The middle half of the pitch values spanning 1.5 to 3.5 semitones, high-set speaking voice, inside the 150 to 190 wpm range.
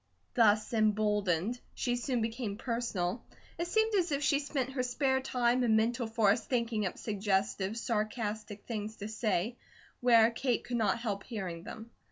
Yes: average, 2.8 semitones; high, 225 Hz; average, 160 wpm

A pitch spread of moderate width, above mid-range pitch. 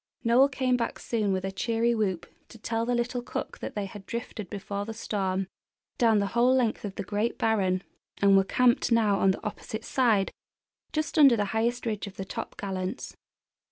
Yes: average, 3.3 semitones; high, 220 Hz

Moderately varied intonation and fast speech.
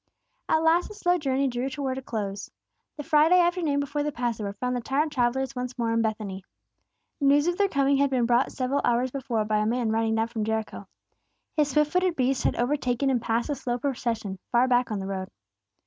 Yes: average, 3.9 semitones; fast, 210 wpm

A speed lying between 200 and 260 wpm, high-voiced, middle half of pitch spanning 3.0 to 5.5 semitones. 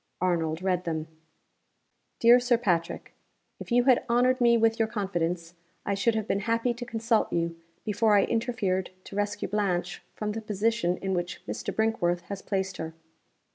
No: average, 170 wpm; high, 205 Hz; average, 4.4 semitones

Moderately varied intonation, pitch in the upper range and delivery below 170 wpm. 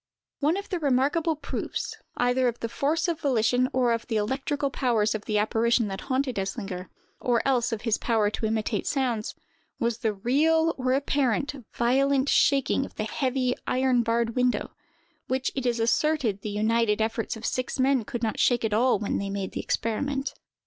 No: average, 3.5 semitones; high, 245 Hz; average, 185 wpm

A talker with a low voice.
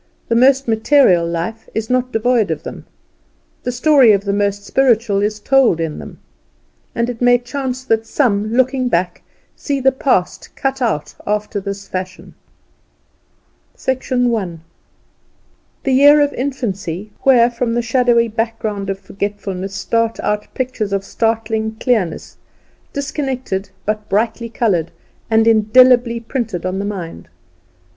No: high, 225 Hz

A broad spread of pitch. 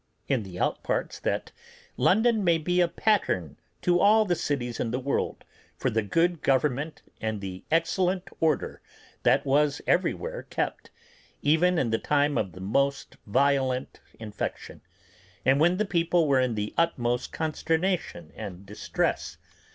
Yes: wide, 7.1 semitones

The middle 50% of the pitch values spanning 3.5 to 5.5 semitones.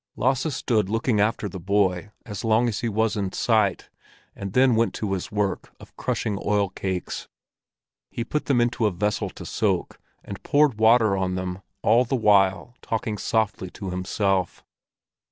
No: average, 3.1 semitones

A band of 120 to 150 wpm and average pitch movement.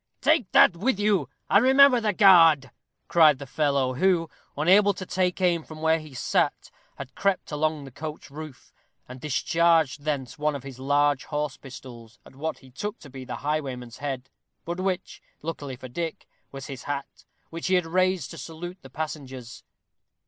No: average, 180 wpm; average, 4.8 semitones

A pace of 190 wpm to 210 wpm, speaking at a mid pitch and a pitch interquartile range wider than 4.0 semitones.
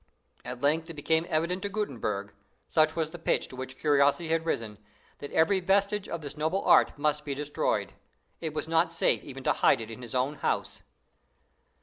No: average, 195 wpm; medium, 155 Hz; average, 3.2 semitones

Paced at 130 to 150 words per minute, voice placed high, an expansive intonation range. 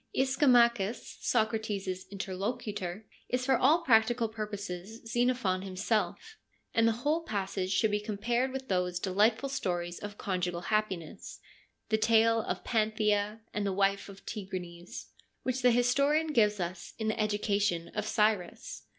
No: average, 140 wpm; high, 215 Hz; average, 3.7 semitones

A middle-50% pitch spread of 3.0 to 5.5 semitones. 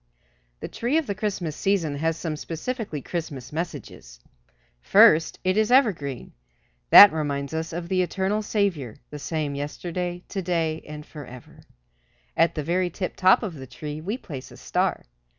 Yes: average, 4.2 semitones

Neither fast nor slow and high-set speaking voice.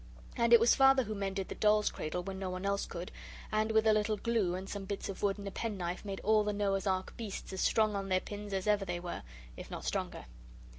No: fast, 255 wpm; high, 200 Hz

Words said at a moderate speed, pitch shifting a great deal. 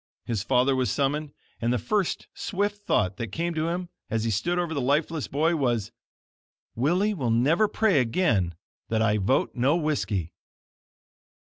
Yes: average, 160 wpm; wide, 6.8 semitones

